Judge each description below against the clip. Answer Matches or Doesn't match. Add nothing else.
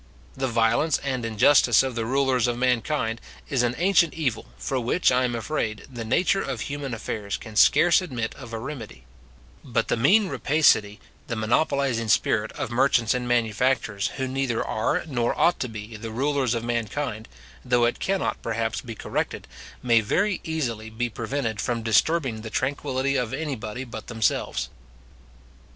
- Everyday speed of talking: Matches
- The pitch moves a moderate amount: Matches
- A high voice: Doesn't match